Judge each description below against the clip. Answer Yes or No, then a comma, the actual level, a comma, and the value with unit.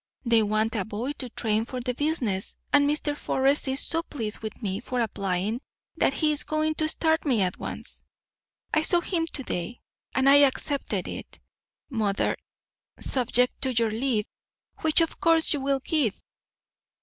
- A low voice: No, very high, 260 Hz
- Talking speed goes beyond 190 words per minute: No, average, 170 wpm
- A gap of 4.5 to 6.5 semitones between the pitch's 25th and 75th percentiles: Yes, average, 5.2 semitones